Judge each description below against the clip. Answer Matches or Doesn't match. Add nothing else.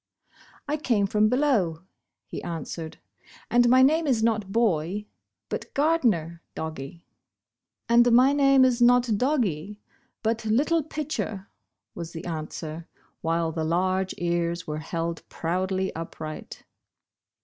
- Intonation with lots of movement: Matches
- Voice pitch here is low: Doesn't match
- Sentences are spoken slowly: Matches